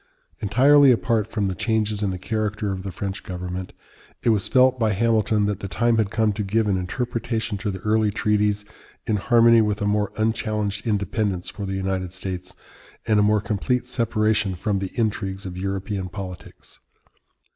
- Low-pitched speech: Yes, low, 105 Hz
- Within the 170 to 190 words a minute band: Yes, average, 180 wpm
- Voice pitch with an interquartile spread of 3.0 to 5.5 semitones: No, narrow, 2.4 semitones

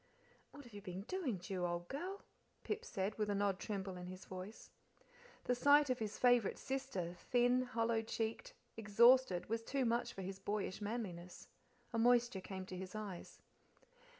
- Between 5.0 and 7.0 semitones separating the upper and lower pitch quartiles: No, average, 4.5 semitones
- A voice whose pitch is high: Yes, high, 215 Hz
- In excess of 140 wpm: Yes, average, 170 wpm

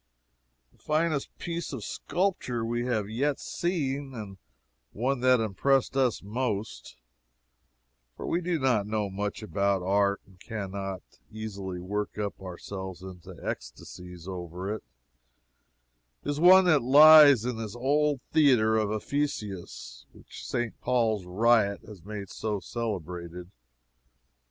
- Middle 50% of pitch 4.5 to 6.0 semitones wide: Yes, wide, 5.4 semitones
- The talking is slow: Yes, slow, 130 wpm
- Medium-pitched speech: No, low, 110 Hz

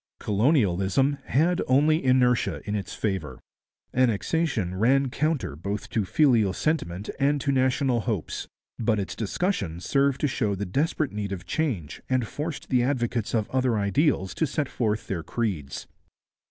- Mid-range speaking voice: No, low, 120 Hz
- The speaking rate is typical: Yes, average, 150 wpm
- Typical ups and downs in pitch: No, wide, 5.8 semitones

